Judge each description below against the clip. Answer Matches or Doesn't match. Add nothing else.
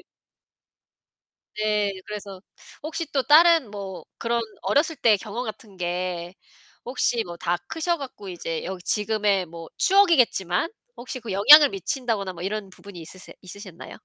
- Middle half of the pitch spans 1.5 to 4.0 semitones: Doesn't match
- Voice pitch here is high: Matches